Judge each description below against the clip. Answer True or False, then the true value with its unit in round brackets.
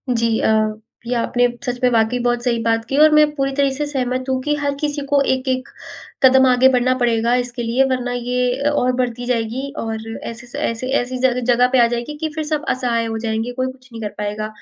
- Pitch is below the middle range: False (250 Hz)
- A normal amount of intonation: False (2.0 semitones)